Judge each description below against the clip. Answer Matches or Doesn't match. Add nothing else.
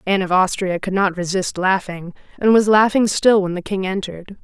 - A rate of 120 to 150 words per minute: Doesn't match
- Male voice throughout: Doesn't match